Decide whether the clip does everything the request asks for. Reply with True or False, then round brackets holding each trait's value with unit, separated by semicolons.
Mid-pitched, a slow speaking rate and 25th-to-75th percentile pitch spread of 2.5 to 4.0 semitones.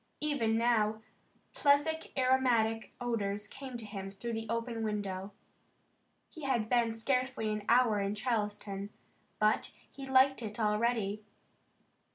False (225 Hz; 125 wpm; 3.2 semitones)